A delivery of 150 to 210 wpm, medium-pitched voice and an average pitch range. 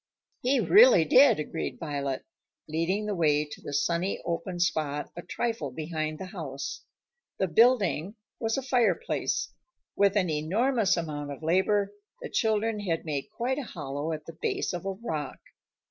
No: average, 160 wpm; medium, 175 Hz; wide, 5.9 semitones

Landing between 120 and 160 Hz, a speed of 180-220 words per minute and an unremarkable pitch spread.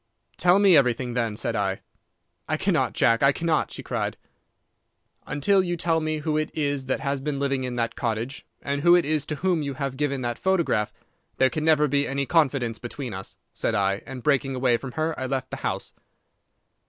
Yes: medium, 140 Hz; fast, 205 wpm; average, 3.9 semitones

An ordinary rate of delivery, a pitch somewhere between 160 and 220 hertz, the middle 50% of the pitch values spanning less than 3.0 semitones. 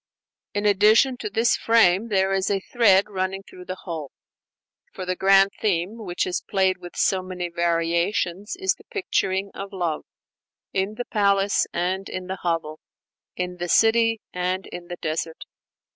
Yes: average, 160 wpm; high, 190 Hz; narrow, 2.4 semitones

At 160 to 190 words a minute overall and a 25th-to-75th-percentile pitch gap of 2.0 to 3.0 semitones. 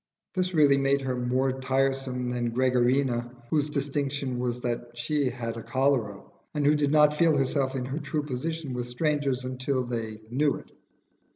Yes: average, 170 wpm; average, 2.7 semitones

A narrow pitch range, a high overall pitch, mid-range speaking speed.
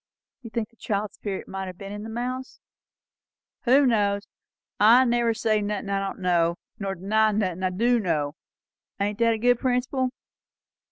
No: average, 3.3 semitones; high, 210 Hz; average, 170 wpm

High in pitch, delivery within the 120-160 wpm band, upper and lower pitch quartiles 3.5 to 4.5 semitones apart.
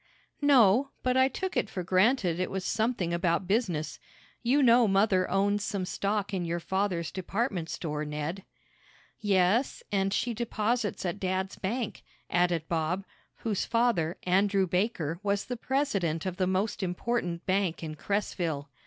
Yes: high, 195 Hz; average, 150 wpm; average, 4.0 semitones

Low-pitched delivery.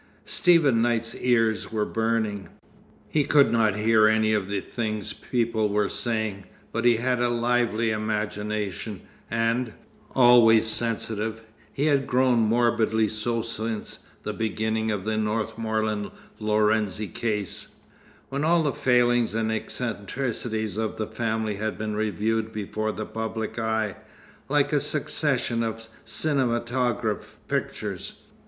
Yes: low, 110 Hz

